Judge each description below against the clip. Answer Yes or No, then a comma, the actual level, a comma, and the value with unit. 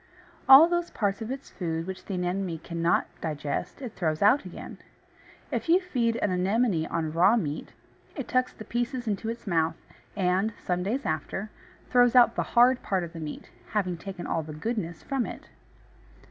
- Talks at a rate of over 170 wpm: Yes, average, 180 wpm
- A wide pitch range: Yes, wide, 6.1 semitones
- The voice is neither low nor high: No, high, 195 Hz